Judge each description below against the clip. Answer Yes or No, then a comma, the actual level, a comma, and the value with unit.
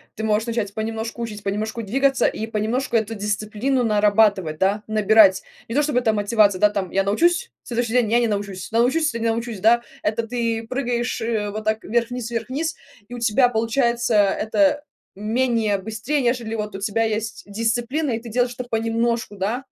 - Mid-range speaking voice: No, high, 225 Hz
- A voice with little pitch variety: Yes, narrow, 2.3 semitones